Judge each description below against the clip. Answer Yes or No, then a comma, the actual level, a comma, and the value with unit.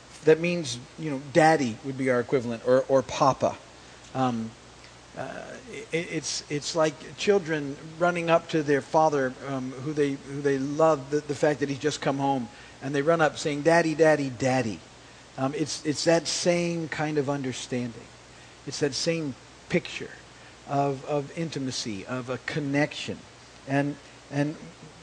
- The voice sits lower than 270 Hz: Yes, medium, 140 Hz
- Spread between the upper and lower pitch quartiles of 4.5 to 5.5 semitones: No, average, 3.4 semitones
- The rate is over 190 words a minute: No, average, 160 wpm